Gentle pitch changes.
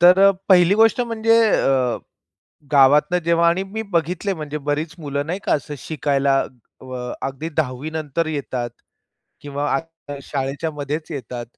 No: average, 3.7 semitones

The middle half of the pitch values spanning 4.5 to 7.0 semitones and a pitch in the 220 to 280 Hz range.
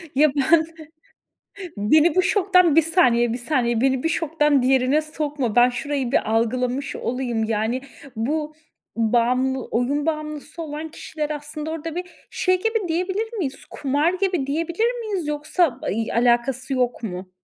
No: average, 4.8 semitones; very high, 290 Hz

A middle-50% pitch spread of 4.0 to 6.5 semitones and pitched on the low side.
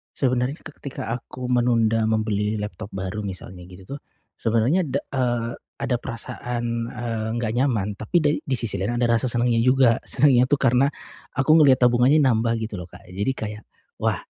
No: average, 2.9 semitones; low, 120 Hz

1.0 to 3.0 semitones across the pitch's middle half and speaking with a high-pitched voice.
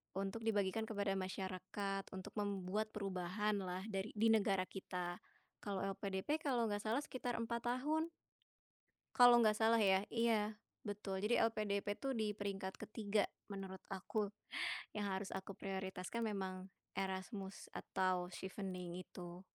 Yes: narrow, 2.4 semitones; high, 200 Hz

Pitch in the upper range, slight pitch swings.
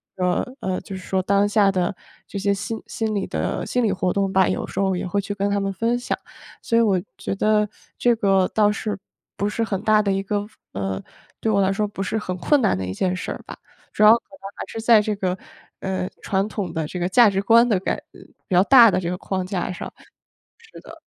Yes: high, 200 Hz; narrow, 2.3 semitones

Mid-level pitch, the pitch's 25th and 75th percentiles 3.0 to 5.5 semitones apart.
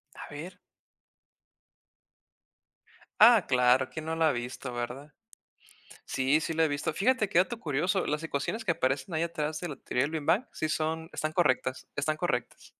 Yes: medium, 155 Hz; average, 3.7 semitones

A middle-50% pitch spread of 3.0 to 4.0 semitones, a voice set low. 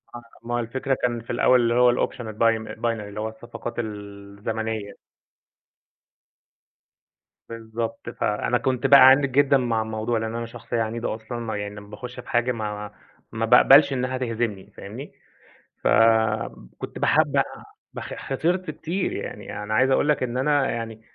No: narrow, 2.5 semitones; low, 115 Hz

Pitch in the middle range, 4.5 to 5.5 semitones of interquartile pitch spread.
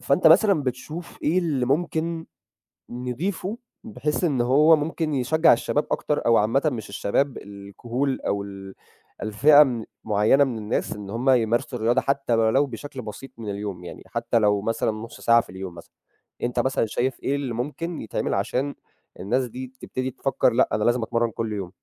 No: low, 125 Hz; average, 4.8 semitones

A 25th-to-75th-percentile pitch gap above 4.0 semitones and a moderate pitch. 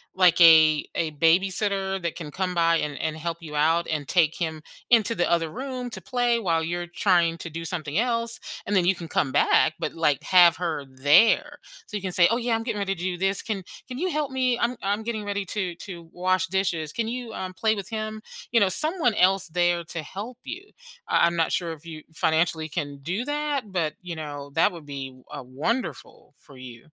Yes: average, 5.2 semitones; medium, 180 Hz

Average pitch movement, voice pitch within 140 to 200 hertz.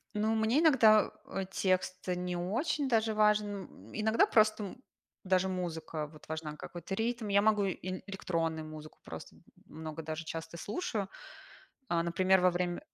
Yes: average, 4.5 semitones; medium, 185 Hz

